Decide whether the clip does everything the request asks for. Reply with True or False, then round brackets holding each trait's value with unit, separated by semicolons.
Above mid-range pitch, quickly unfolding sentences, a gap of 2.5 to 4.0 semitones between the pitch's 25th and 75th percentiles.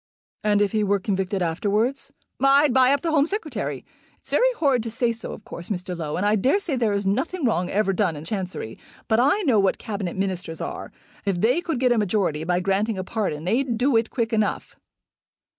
False (215 Hz; 215 wpm; 5.2 semitones)